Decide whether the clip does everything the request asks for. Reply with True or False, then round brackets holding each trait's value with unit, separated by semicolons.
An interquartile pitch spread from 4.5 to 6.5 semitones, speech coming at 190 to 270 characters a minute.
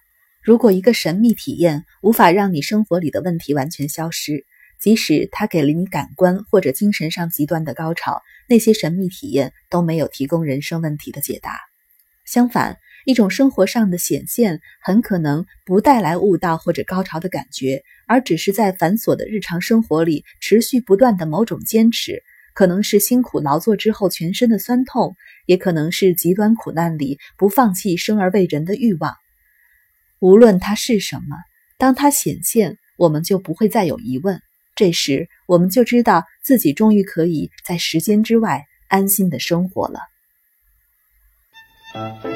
True (5.4 semitones; 255 characters per minute)